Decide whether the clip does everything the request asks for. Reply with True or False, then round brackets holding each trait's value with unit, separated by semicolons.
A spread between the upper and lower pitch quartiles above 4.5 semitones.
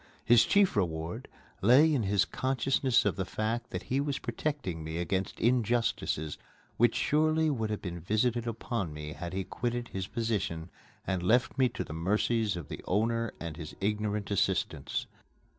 True (5.0 semitones)